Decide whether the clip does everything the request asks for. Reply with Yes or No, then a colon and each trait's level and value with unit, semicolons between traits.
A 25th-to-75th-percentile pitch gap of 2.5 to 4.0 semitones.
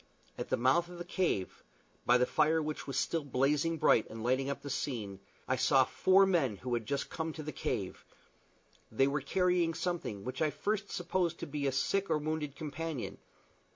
No: average, 4.6 semitones